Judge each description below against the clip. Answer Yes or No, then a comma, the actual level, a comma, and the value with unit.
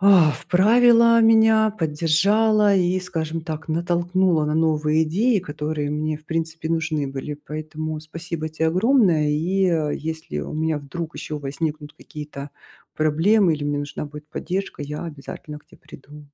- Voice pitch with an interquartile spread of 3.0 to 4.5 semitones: Yes, average, 3.4 semitones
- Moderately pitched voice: Yes, medium, 160 Hz